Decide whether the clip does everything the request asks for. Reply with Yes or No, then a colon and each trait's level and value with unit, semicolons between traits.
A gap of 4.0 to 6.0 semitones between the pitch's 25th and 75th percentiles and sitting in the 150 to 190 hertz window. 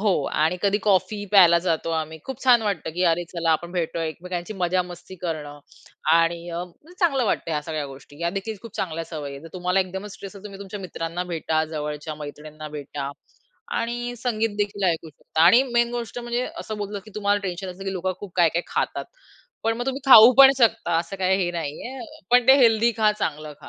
Yes: average, 4.7 semitones; medium, 185 Hz